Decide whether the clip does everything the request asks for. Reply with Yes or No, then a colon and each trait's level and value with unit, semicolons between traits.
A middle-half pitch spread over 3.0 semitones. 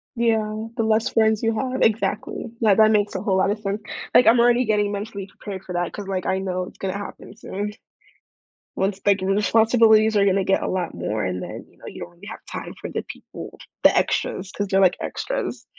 No: narrow, 2.5 semitones